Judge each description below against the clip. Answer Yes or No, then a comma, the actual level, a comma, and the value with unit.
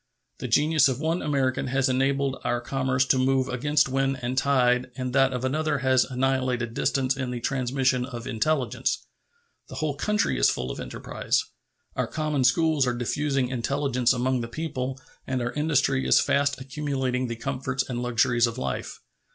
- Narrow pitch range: Yes, narrow, 1.8 semitones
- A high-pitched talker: No, low, 130 Hz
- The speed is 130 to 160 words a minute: No, average, 170 wpm